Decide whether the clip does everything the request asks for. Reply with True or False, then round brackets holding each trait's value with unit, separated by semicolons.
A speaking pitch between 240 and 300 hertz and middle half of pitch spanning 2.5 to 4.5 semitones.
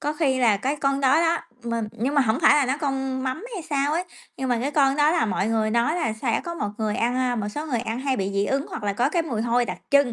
True (260 Hz; 4.1 semitones)